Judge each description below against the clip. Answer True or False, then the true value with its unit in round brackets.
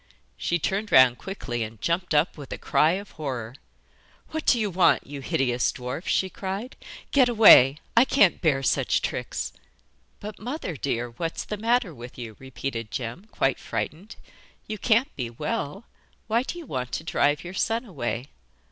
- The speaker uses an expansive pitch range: True (8.8 semitones)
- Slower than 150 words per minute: False (170 wpm)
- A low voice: False (160 Hz)